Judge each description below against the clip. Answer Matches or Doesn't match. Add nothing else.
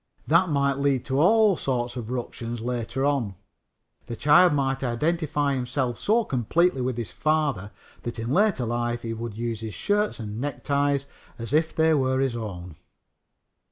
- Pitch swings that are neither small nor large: Matches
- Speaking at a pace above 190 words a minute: Doesn't match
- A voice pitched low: Matches